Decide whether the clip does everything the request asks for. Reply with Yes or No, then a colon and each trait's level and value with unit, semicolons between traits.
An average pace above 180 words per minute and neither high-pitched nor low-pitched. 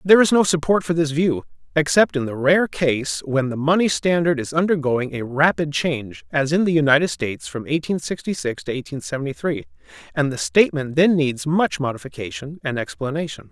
Yes: average, 190 wpm; medium, 145 Hz